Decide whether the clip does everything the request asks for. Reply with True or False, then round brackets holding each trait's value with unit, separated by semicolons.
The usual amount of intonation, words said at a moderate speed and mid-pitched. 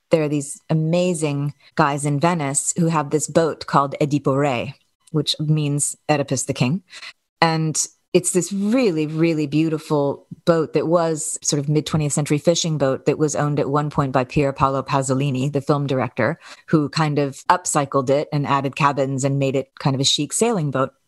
False (2.3 semitones; 180 wpm; 150 Hz)